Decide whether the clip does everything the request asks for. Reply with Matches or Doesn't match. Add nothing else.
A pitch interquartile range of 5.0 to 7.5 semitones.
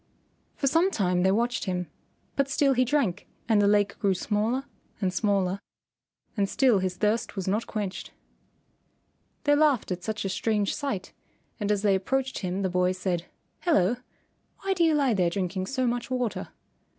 Matches